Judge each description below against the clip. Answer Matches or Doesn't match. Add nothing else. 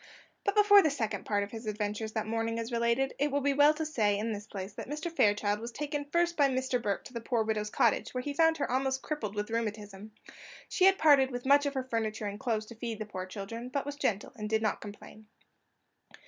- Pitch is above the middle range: Matches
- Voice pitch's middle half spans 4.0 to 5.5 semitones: Matches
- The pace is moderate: Doesn't match